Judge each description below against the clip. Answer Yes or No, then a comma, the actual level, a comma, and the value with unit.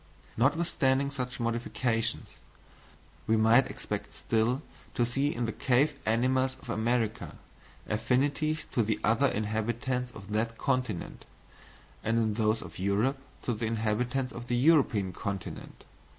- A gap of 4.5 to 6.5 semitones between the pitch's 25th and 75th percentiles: No, average, 2.9 semitones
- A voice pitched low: Yes, low, 120 Hz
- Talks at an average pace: No, slow, 130 wpm